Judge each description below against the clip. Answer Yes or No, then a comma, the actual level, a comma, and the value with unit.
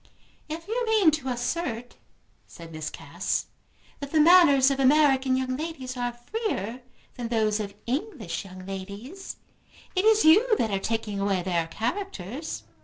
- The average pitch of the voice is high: Yes, very high, 255 Hz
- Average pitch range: No, wide, 7.6 semitones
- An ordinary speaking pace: Yes, average, 150 wpm